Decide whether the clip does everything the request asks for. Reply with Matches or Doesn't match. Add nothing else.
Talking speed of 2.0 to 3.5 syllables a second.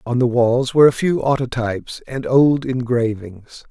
Doesn't match